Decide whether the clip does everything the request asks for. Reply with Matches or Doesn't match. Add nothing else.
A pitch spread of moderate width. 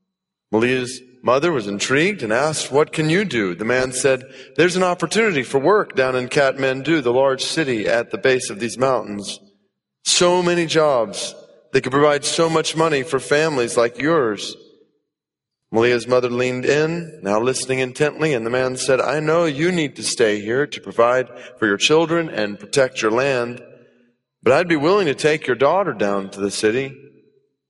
Matches